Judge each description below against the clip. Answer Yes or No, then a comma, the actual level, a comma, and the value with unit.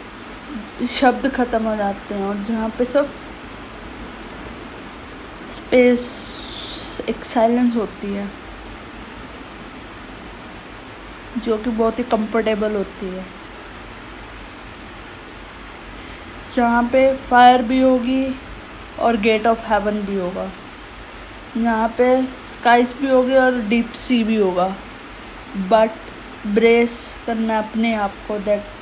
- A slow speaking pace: Yes, slow, 100 wpm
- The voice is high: Yes, high, 230 Hz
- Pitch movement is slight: Yes, narrow, 2.3 semitones